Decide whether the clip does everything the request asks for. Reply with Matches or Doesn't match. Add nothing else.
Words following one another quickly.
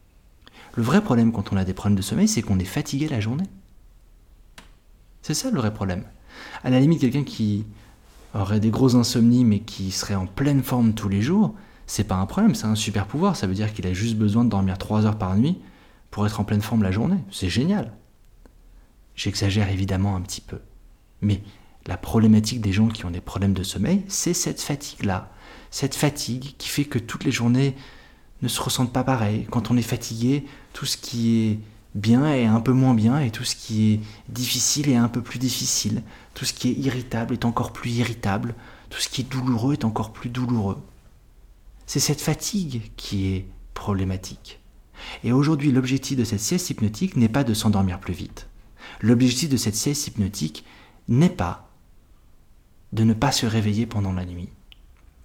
Doesn't match